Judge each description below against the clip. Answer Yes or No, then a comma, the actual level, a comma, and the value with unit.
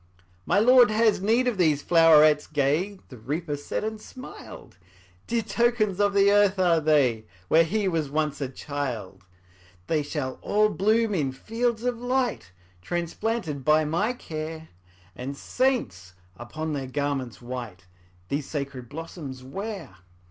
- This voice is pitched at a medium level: Yes, medium, 160 Hz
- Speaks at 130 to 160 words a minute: Yes, average, 140 wpm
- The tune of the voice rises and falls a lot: Yes, wide, 7.3 semitones